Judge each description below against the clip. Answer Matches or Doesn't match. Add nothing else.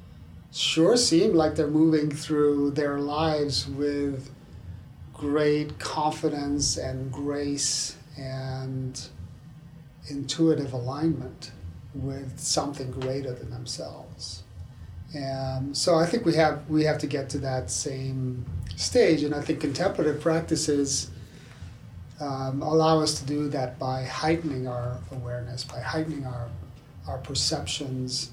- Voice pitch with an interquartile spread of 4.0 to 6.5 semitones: Doesn't match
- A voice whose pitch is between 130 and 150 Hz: Matches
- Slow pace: Matches